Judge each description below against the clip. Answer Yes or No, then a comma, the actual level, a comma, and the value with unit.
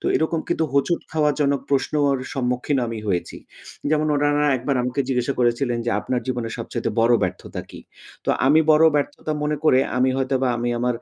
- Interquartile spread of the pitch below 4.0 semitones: Yes, average, 3.1 semitones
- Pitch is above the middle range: No, low, 135 Hz